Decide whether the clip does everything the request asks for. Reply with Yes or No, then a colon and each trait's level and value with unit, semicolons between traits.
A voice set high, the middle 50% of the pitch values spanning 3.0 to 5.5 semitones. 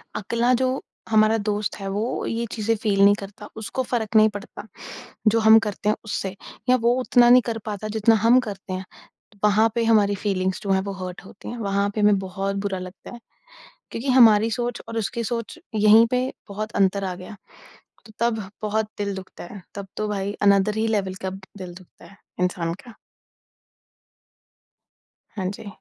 No: high, 210 Hz; narrow, 2.5 semitones